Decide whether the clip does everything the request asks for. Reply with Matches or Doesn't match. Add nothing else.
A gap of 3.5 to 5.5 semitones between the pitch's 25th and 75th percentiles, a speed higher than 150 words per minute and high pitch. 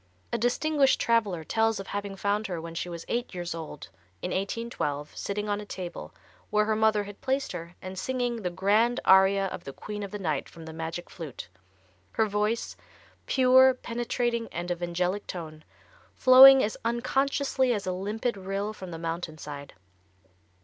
Matches